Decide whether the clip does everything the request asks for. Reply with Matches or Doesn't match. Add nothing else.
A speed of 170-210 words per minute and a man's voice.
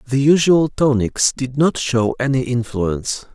Doesn't match